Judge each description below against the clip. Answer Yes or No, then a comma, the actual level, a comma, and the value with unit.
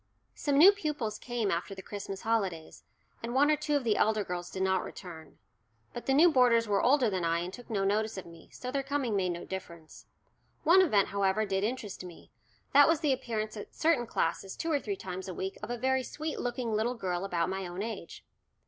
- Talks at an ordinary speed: No, fast, 220 wpm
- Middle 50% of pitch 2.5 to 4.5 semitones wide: No, wide, 5.6 semitones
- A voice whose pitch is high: Yes, high, 215 Hz